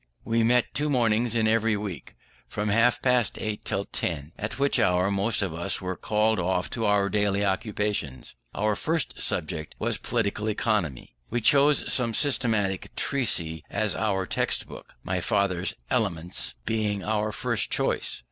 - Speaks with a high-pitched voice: No, low, 105 Hz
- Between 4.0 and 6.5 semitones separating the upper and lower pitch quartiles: No, average, 3.2 semitones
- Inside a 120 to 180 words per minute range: Yes, average, 155 wpm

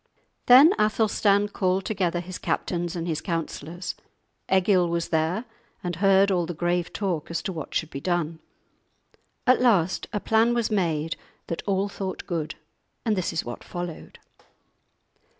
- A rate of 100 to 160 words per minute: Yes, average, 150 wpm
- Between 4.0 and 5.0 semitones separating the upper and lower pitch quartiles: No, average, 3.2 semitones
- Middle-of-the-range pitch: Yes, medium, 180 Hz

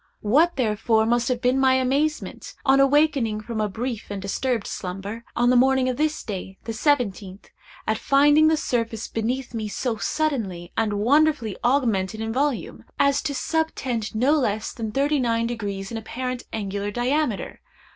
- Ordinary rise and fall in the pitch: Yes, average, 4.2 semitones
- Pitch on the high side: Yes, high, 240 Hz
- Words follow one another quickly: No, average, 165 wpm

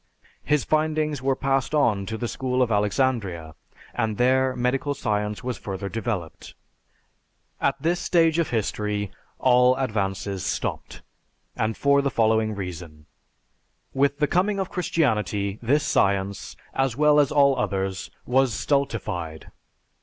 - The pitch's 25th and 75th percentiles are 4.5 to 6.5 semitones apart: Yes, wide, 5.4 semitones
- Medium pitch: No, low, 125 Hz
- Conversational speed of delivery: No, slow, 130 wpm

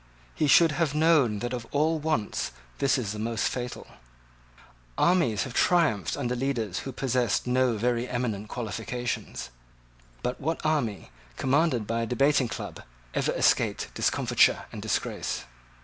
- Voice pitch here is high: No, low, 125 Hz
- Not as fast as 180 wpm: Yes, average, 140 wpm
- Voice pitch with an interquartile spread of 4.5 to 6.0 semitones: No, average, 4.1 semitones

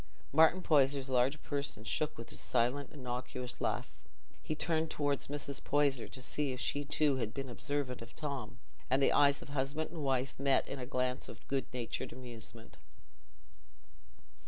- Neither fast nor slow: Yes, average, 165 wpm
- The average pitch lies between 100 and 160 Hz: Yes, low, 135 Hz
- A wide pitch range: No, narrow, 2.4 semitones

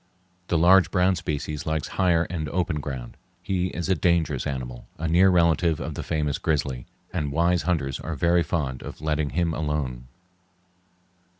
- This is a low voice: Yes, very low, 80 Hz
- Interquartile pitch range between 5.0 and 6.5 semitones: No, average, 3.2 semitones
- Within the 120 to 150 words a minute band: No, average, 165 wpm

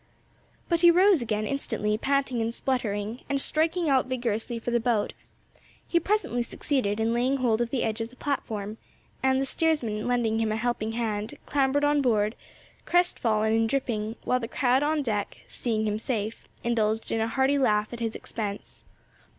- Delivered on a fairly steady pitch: No, average, 3.7 semitones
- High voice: Yes, high, 235 Hz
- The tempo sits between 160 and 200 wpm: Yes, average, 175 wpm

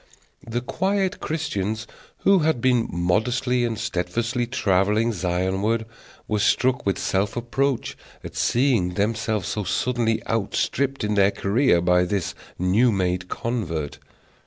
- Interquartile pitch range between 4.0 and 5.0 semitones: Yes, average, 4.4 semitones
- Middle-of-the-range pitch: No, low, 110 Hz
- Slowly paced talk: Yes, slow, 125 wpm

